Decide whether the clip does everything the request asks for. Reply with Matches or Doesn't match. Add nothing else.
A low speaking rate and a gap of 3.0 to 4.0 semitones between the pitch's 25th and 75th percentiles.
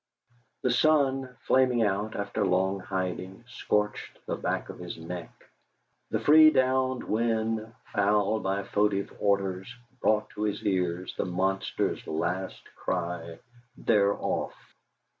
Matches